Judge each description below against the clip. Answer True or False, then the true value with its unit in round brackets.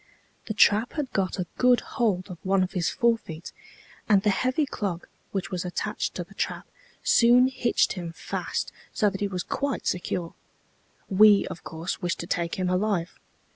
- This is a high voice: True (195 Hz)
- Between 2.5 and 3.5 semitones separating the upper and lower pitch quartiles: False (4.2 semitones)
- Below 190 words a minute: True (175 wpm)